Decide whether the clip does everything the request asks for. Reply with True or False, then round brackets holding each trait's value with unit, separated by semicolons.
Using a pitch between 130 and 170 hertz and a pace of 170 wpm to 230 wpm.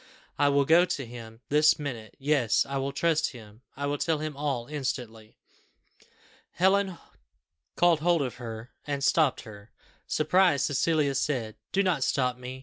False (140 Hz; 155 wpm)